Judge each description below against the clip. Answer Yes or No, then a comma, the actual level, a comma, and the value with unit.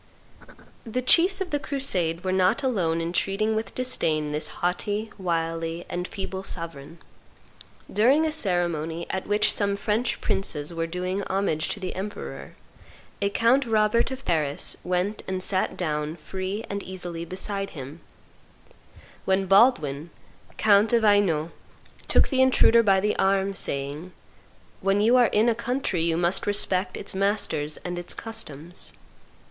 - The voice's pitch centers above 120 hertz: Yes, high, 190 Hz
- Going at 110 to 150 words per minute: Yes, average, 145 wpm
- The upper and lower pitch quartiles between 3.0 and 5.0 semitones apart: Yes, average, 4.2 semitones